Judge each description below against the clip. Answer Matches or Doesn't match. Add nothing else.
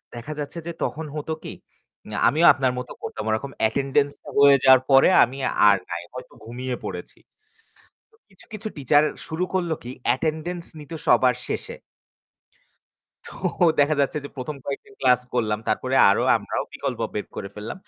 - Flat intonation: Doesn't match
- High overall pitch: Doesn't match